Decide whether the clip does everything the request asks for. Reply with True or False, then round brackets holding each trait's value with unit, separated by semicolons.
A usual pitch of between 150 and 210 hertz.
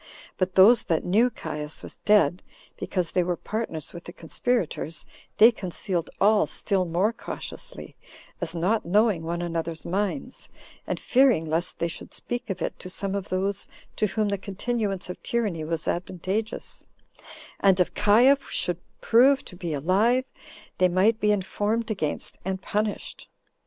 True (190 Hz)